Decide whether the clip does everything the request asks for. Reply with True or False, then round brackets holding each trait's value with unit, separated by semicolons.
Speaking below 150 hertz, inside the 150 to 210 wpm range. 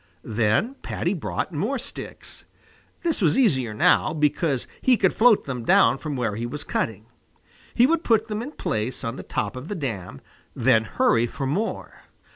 True (140 Hz; 175 wpm)